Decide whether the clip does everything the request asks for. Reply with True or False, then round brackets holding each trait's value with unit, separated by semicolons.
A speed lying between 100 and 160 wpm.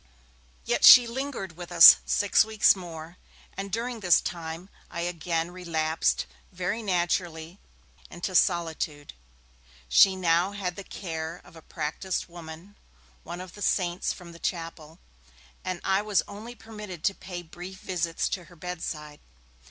True (145 wpm)